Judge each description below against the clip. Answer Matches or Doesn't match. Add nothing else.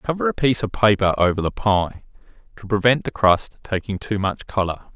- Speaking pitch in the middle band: Doesn't match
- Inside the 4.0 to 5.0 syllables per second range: Doesn't match